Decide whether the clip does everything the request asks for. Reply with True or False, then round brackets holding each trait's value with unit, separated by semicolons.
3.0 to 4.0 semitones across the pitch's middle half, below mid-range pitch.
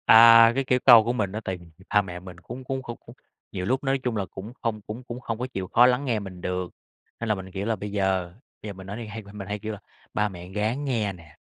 True (3.7 semitones; 105 Hz)